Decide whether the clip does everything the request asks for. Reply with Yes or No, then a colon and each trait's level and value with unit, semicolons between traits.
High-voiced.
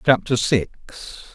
No: low, 110 Hz